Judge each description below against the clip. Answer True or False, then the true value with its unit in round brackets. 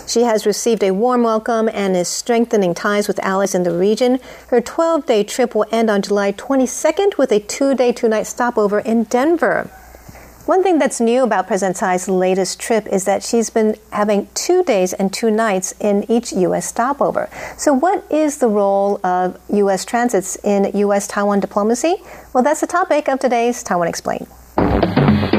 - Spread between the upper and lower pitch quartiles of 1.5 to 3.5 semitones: False (4.0 semitones)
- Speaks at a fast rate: False (180 wpm)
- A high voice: True (225 Hz)